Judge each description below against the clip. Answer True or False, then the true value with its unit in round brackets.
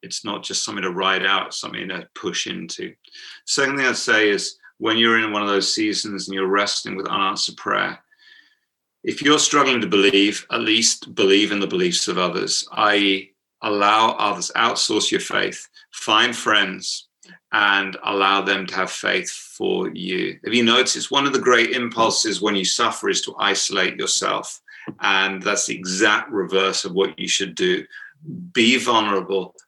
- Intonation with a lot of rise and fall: True (6.0 semitones)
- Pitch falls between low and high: False (105 Hz)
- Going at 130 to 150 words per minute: False (170 wpm)